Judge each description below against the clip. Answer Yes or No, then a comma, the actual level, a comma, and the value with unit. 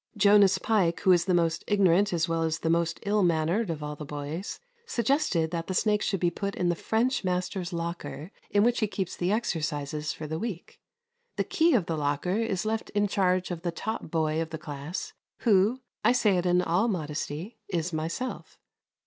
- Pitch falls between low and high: Yes, medium, 180 Hz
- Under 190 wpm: No, average, 200 wpm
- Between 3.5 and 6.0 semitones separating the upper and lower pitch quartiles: Yes, average, 4.1 semitones